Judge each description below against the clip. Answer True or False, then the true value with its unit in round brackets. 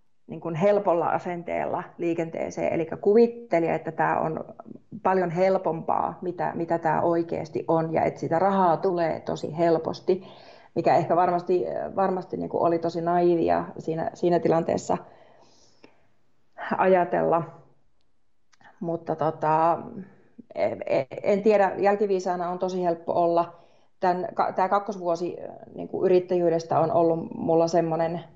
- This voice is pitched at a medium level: True (175 Hz)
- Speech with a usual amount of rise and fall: False (2.2 semitones)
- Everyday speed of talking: True (120 wpm)